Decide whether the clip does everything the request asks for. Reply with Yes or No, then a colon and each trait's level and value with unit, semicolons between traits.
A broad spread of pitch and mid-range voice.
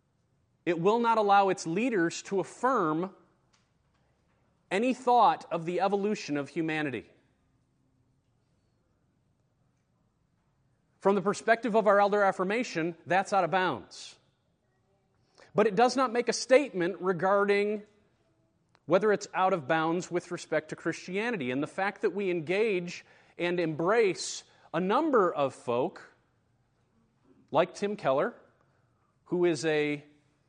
No: average, 4.8 semitones; medium, 175 Hz